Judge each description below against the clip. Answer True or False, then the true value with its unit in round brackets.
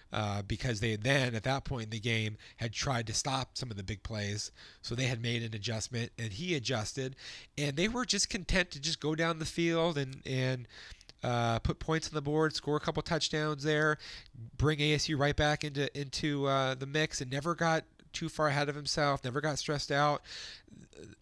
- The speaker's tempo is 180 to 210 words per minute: True (205 wpm)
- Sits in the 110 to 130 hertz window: False (140 Hz)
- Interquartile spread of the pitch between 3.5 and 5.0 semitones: True (4.5 semitones)